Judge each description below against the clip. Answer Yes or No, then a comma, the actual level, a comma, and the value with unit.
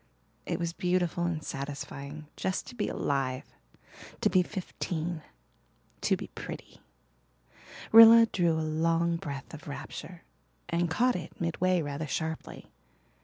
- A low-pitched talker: No, medium, 165 Hz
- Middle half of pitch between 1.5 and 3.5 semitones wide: Yes, narrow, 2.6 semitones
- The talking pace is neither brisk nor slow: No, slow, 125 wpm